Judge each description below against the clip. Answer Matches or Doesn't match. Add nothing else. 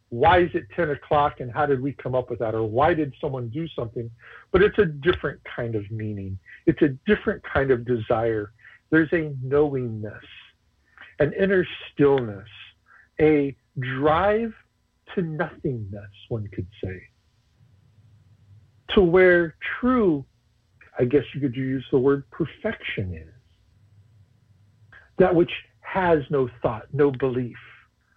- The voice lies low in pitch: Matches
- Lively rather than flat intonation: Matches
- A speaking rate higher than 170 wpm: Doesn't match